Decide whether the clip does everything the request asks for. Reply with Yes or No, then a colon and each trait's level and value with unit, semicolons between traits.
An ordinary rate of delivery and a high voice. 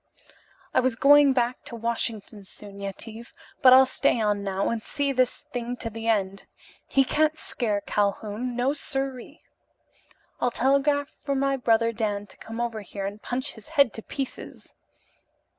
Yes: average, 170 wpm; high, 235 Hz